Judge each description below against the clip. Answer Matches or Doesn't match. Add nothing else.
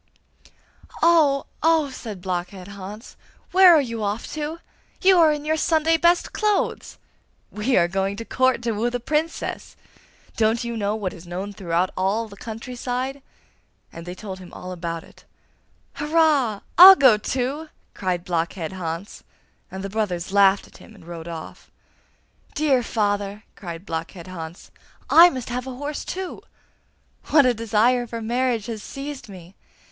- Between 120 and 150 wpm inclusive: Doesn't match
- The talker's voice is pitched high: Matches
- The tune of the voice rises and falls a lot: Matches